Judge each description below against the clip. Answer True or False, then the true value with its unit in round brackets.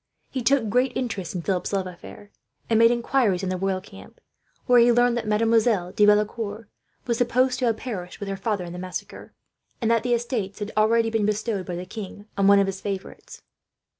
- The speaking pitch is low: False (215 Hz)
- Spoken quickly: True (210 wpm)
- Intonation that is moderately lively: True (3.3 semitones)